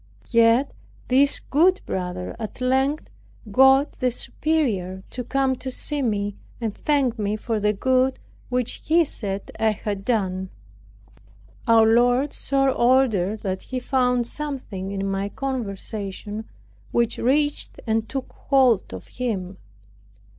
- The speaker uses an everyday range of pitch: Yes, average, 4.6 semitones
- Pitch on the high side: Yes, high, 235 Hz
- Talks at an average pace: No, slow, 130 wpm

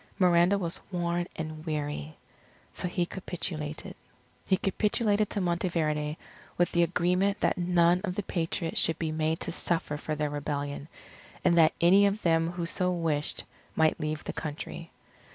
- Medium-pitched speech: Yes, medium, 170 Hz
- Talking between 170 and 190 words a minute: No, average, 155 wpm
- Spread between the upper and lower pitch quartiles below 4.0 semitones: Yes, narrow, 2.5 semitones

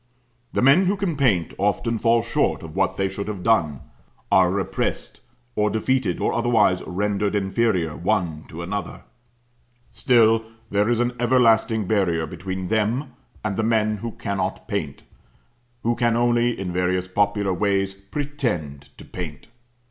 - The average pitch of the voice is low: Yes, low, 105 Hz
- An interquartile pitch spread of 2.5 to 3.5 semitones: No, average, 4.1 semitones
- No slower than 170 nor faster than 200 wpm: No, average, 150 wpm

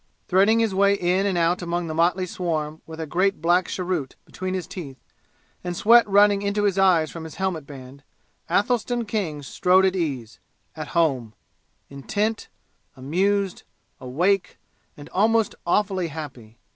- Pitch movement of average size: Yes, average, 4.1 semitones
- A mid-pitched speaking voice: Yes, medium, 180 Hz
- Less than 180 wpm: Yes, average, 150 wpm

